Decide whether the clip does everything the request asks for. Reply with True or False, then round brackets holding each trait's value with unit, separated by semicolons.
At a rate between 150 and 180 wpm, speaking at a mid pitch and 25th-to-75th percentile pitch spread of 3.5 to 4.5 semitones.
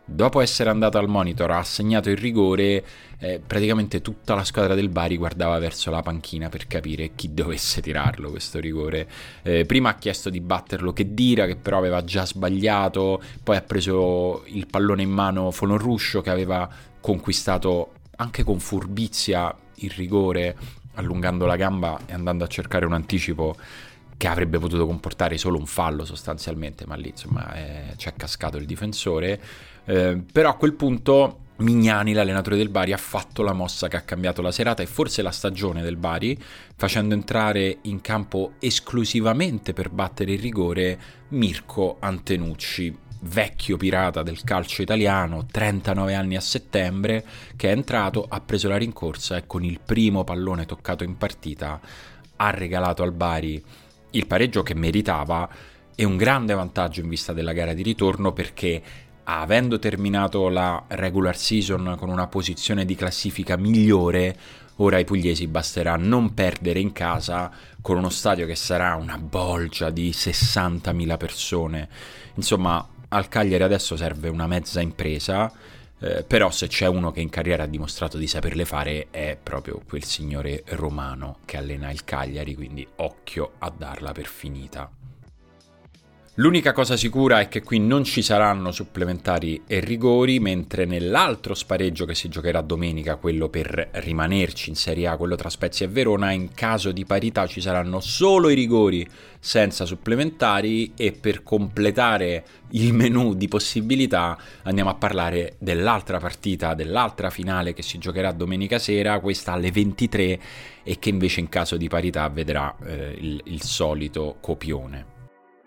False (155 wpm; 95 Hz; 3.8 semitones)